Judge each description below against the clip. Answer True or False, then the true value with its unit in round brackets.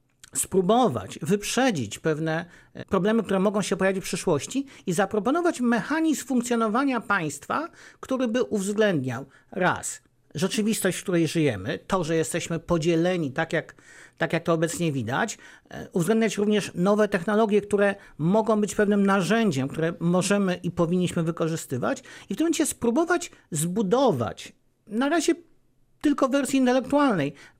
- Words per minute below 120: False (130 wpm)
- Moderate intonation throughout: False (5.9 semitones)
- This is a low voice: False (200 Hz)